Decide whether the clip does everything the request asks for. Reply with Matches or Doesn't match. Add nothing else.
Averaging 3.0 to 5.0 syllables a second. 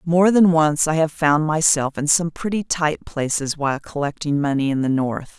Matches